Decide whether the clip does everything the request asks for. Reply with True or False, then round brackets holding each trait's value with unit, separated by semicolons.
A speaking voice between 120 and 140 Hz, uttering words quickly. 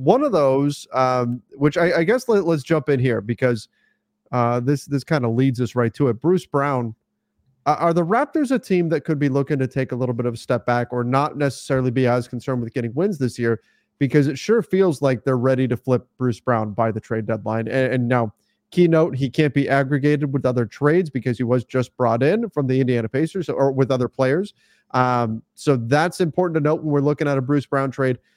True (135 Hz; 235 wpm)